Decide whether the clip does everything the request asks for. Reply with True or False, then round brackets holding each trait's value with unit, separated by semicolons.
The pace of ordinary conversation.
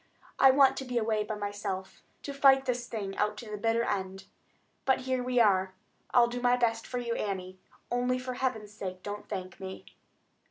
True (195 wpm)